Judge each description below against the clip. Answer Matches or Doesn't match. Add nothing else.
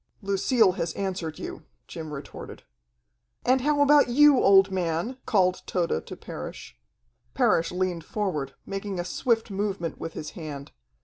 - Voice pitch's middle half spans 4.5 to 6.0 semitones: Matches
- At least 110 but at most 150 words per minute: Matches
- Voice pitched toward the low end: Doesn't match